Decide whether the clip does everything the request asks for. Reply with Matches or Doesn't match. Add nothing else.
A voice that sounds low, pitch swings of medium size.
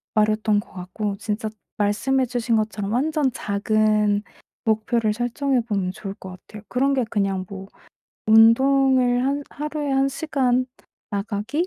Doesn't match